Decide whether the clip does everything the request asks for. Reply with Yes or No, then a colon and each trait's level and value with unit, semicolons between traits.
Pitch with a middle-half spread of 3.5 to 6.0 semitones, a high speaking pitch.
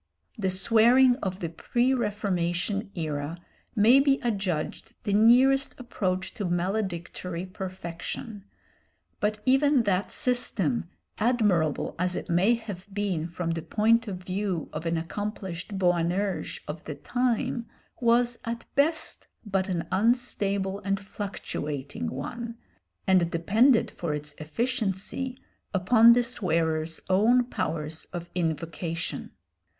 Yes: average, 5.3 semitones; high, 195 Hz